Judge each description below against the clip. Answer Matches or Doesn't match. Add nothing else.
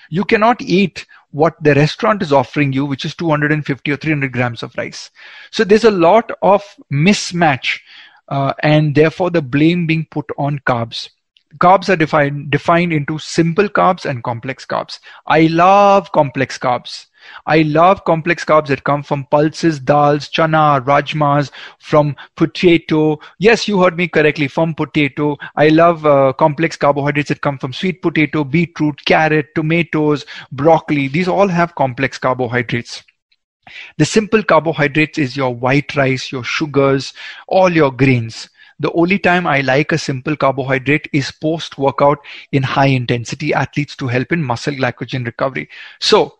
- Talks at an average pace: Matches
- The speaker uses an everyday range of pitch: Matches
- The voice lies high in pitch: Doesn't match